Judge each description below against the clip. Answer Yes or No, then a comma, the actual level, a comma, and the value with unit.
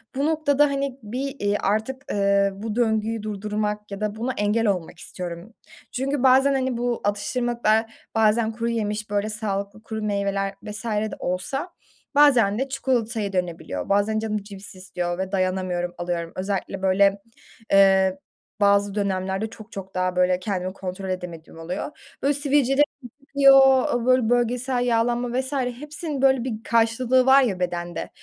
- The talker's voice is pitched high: Yes, high, 215 Hz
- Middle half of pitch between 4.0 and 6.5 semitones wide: Yes, average, 4.3 semitones